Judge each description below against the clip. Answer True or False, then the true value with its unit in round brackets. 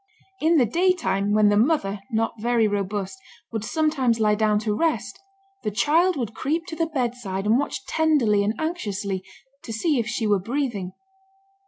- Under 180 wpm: True (170 wpm)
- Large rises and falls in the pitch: True (6.5 semitones)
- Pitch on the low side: False (225 Hz)